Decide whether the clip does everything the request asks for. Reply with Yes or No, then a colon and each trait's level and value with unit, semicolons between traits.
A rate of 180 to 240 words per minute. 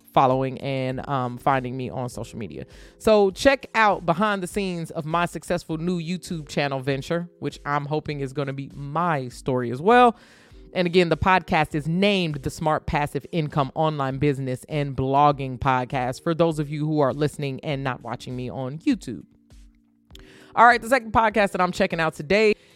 Yes: average, 185 wpm